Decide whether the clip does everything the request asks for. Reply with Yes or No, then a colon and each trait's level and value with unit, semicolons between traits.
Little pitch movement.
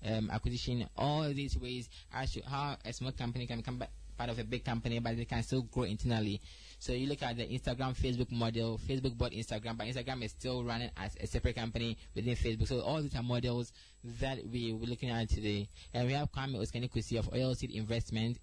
Yes: narrow, 2.0 semitones